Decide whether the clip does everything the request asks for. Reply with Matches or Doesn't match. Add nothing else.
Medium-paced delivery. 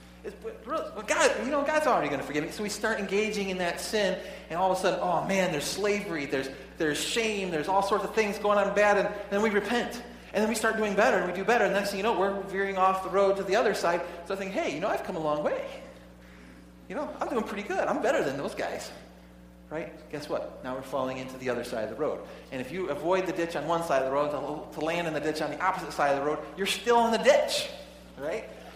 Doesn't match